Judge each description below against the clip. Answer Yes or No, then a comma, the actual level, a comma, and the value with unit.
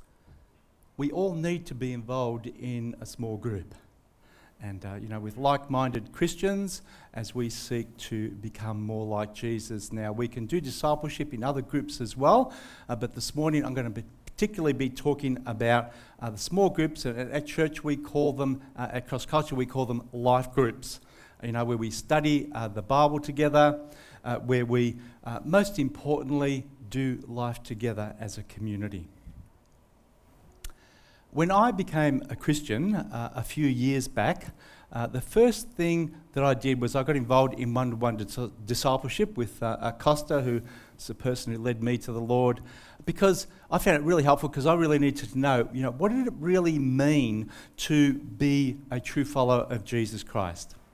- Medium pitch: No, low, 125 Hz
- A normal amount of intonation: Yes, average, 3.9 semitones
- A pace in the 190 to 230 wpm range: No, average, 180 wpm